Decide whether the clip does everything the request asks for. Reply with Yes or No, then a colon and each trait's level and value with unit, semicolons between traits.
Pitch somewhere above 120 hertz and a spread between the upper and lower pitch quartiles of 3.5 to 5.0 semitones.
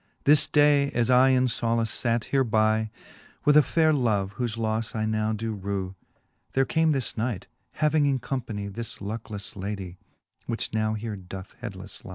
No: low, 115 Hz; average, 4.1 semitones